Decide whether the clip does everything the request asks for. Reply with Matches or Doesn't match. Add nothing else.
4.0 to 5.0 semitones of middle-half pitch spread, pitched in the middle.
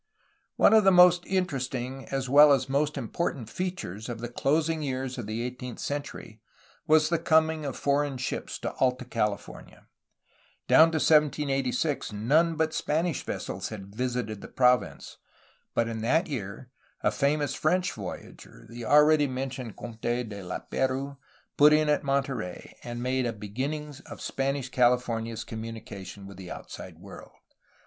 Doesn't match